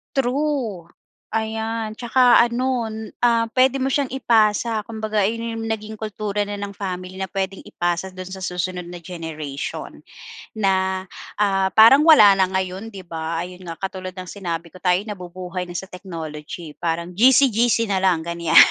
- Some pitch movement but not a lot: Yes, average, 3.8 semitones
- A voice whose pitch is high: Yes, high, 195 Hz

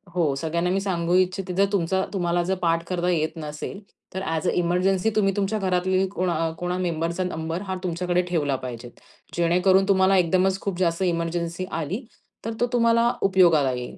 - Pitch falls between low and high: Yes, medium, 180 Hz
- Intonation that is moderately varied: No, narrow, 2.2 semitones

